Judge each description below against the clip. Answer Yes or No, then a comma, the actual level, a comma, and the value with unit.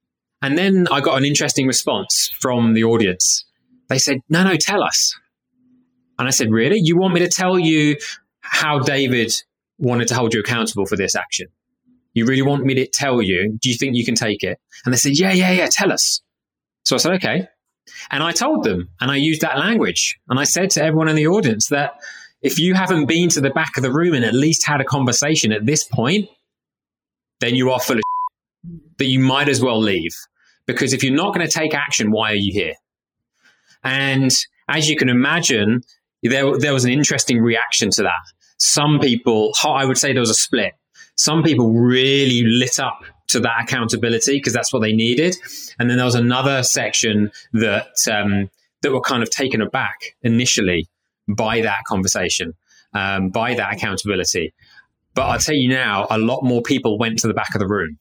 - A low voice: Yes, low, 130 Hz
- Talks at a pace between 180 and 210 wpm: Yes, average, 200 wpm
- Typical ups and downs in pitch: Yes, average, 4.8 semitones